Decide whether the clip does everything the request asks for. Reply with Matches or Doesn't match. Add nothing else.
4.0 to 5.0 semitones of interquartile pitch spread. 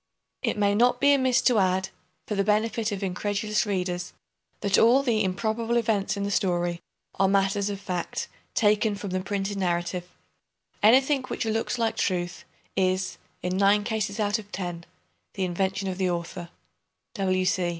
Doesn't match